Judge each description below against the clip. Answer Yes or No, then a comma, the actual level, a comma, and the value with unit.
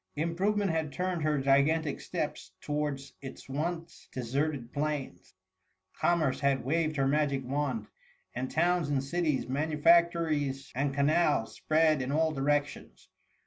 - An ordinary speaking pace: No, slow, 130 wpm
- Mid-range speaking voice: Yes, medium, 150 Hz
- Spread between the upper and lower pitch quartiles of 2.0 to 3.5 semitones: Yes, average, 2.9 semitones